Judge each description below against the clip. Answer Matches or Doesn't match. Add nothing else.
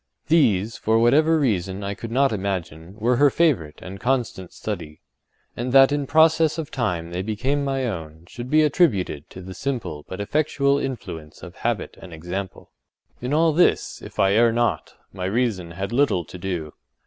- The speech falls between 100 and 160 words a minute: Doesn't match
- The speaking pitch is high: Doesn't match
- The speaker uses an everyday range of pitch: Doesn't match